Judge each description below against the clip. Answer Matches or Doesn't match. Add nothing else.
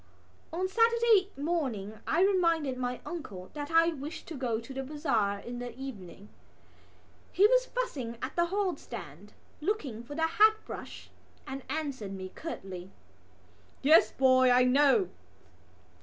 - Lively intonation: Matches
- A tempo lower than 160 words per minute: Matches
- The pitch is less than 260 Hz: Doesn't match